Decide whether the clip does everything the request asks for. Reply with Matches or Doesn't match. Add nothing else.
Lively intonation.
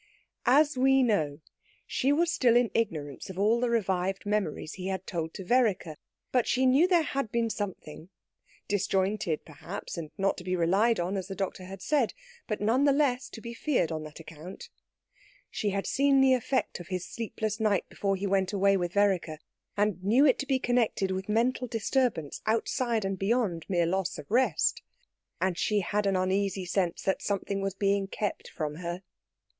Doesn't match